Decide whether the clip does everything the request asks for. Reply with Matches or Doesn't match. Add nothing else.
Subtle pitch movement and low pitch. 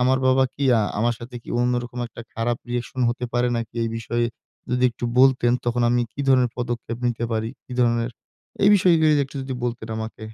Matches